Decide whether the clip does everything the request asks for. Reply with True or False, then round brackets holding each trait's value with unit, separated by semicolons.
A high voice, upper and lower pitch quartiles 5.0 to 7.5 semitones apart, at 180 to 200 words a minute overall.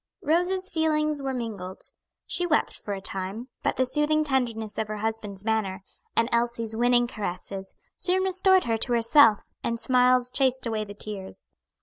False (235 Hz; 5.3 semitones; 160 wpm)